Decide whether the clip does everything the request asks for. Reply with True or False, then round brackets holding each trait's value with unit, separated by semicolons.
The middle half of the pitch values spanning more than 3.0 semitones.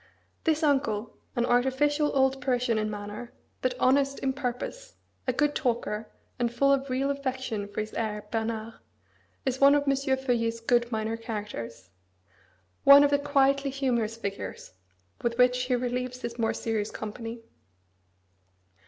True (3.4 semitones)